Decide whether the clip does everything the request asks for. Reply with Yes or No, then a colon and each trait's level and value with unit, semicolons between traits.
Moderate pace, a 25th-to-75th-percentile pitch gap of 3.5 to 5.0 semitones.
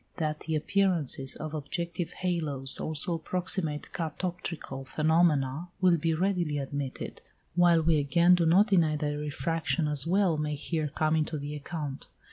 No: average, 145 wpm; average, 2.7 semitones